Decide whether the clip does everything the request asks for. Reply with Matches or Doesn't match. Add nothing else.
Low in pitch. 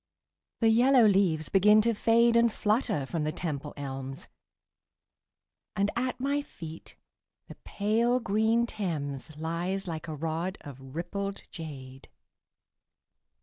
Doesn't match